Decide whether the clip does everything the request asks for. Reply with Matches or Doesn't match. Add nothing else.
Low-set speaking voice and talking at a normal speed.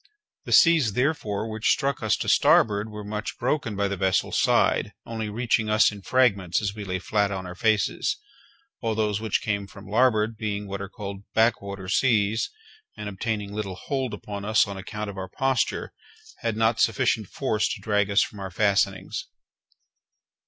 Matches